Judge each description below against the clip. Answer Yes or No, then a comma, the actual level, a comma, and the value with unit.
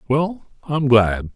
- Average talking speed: Yes, average, 180 wpm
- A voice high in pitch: No, low, 135 Hz